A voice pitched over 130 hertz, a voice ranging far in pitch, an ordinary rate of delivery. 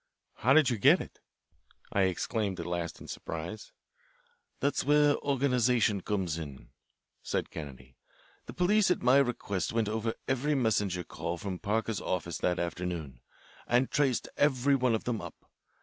No: low, 110 Hz; wide, 6.8 semitones; average, 150 wpm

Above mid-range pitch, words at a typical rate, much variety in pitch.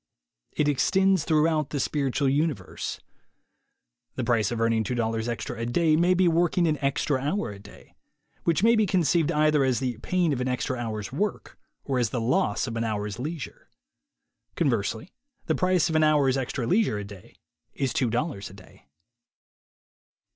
No: low, 135 Hz; average, 170 wpm; wide, 5.9 semitones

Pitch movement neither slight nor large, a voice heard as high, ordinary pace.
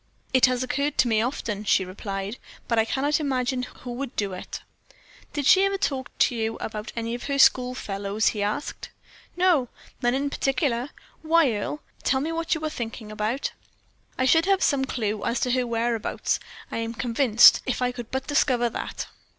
Yes: average, 3.7 semitones; very high, 250 Hz; average, 185 wpm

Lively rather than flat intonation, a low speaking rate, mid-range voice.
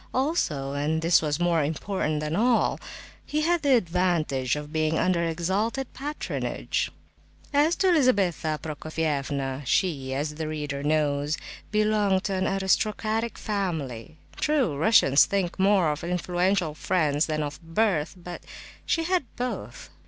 Yes: wide, 5.8 semitones; slow, 130 wpm; medium, 170 Hz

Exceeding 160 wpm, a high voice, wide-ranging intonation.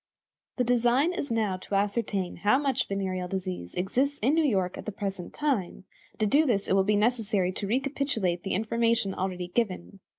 No: average, 190 wpm; high, 205 Hz; average, 4.5 semitones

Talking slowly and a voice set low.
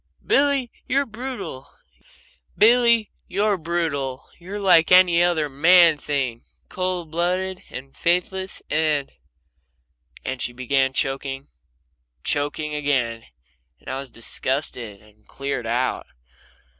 No: slow, 100 wpm; medium, 150 Hz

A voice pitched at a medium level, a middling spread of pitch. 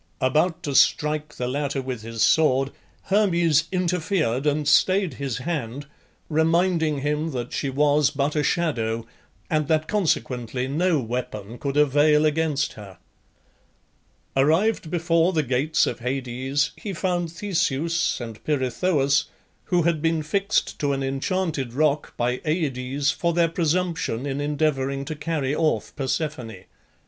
Yes: medium, 150 Hz; average, 3.7 semitones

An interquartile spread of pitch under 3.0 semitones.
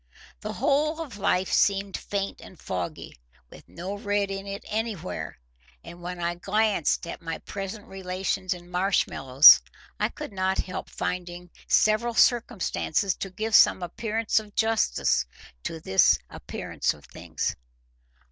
No: average, 3.3 semitones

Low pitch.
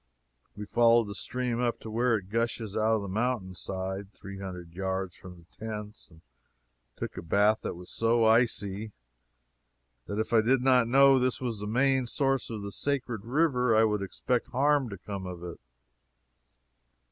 Yes: low, 110 Hz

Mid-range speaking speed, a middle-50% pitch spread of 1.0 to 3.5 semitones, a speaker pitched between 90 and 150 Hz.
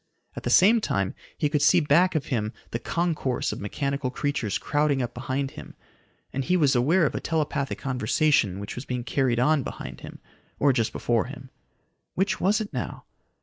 No: average, 190 wpm; average, 3.9 semitones; medium, 140 Hz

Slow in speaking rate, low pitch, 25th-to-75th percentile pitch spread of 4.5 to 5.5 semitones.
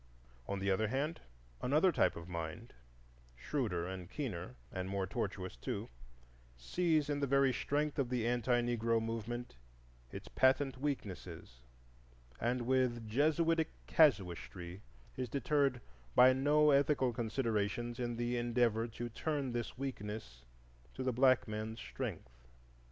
Yes: slow, 130 wpm; low, 120 Hz; average, 4.8 semitones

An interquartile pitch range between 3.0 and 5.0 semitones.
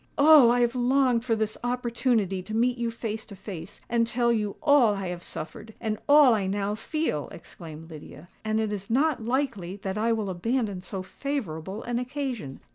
Yes: average, 4.0 semitones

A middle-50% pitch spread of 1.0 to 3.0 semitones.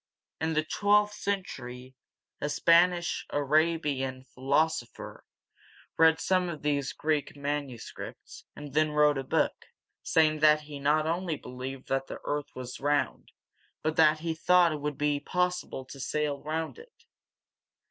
Yes: narrow, 2.5 semitones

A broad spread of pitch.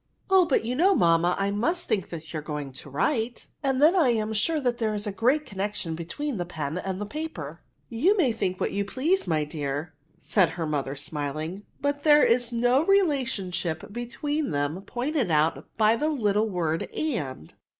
Yes: wide, 8.8 semitones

